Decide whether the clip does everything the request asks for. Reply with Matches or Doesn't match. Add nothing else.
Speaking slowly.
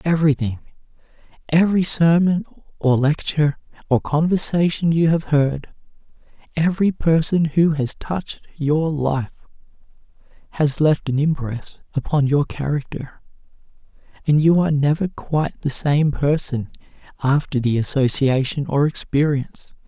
Matches